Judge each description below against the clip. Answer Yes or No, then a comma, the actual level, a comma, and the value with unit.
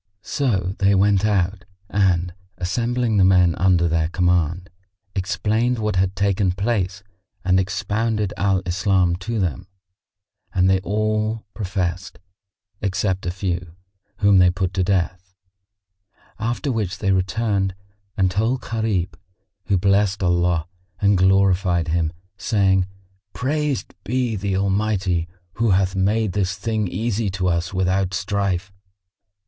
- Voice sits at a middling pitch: No, very low, 95 Hz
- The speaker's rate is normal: No, slow, 125 wpm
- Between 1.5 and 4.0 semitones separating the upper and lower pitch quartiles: Yes, narrow, 2.4 semitones